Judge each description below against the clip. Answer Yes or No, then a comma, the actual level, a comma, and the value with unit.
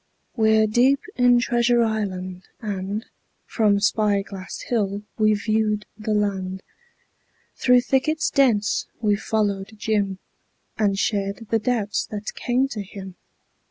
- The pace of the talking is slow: Yes, slow, 125 wpm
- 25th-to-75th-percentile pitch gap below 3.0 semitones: Yes, narrow, 2.6 semitones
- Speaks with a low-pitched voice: No, high, 215 Hz